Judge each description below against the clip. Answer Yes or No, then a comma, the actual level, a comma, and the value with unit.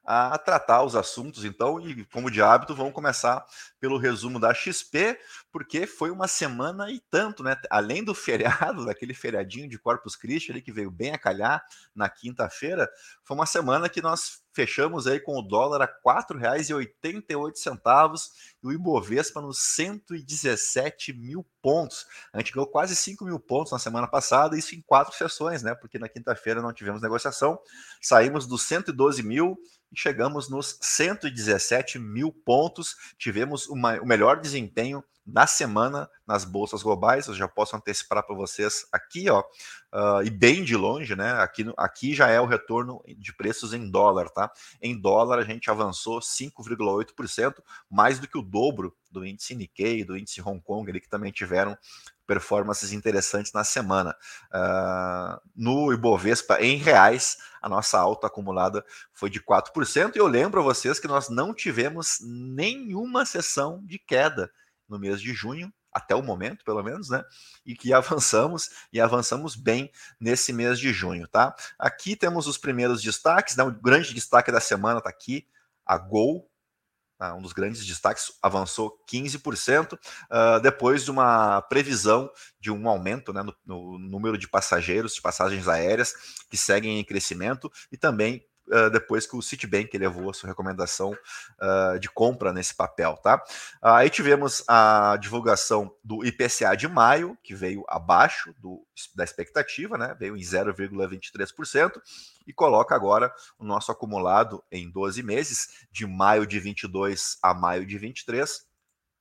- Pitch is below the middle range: Yes, low, 115 Hz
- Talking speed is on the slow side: No, average, 160 wpm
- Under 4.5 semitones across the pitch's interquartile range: No, wide, 5.5 semitones